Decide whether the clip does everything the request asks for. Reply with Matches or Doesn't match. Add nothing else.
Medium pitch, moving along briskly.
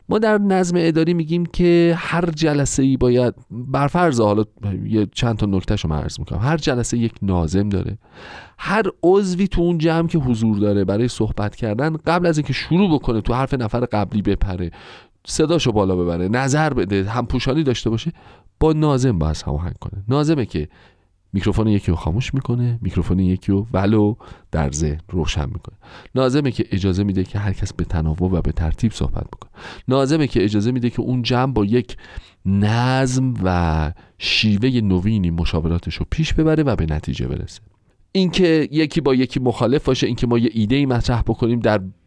Doesn't match